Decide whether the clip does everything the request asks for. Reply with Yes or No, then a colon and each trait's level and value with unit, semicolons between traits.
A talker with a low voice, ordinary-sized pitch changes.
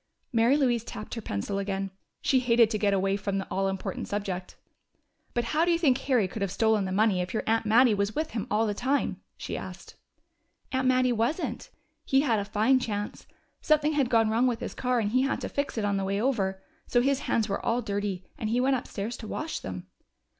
No: high, 225 Hz; average, 4.1 semitones